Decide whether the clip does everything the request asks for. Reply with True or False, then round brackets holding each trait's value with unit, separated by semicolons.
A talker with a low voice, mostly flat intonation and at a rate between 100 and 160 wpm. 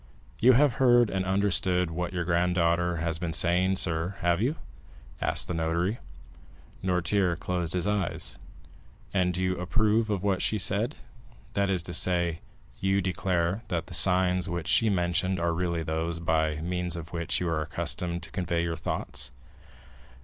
True (90 Hz; 2.2 semitones; 155 wpm)